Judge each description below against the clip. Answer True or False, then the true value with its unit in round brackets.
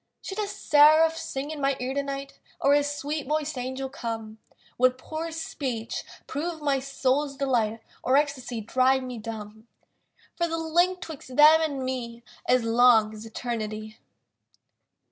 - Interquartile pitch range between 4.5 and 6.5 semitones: False (4.1 semitones)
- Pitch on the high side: True (270 Hz)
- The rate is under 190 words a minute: True (145 wpm)